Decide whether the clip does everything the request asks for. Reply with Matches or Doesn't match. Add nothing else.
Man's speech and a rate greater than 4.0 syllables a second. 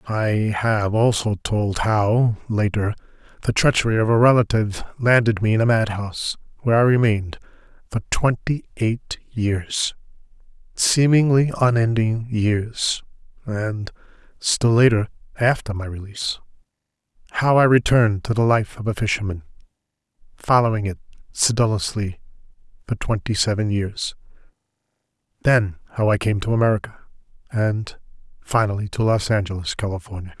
Matches